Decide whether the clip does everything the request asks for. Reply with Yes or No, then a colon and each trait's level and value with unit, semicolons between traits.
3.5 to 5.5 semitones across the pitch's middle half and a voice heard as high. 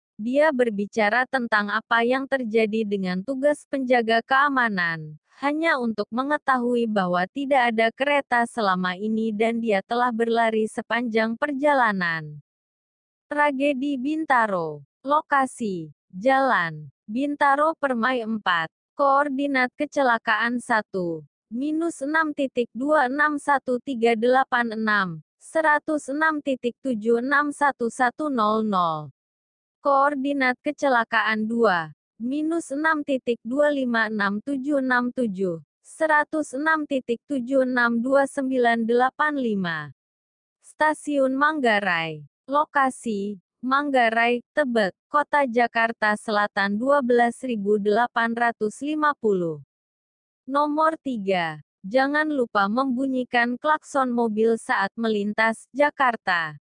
Yes: average, 4.7 semitones; high, 245 Hz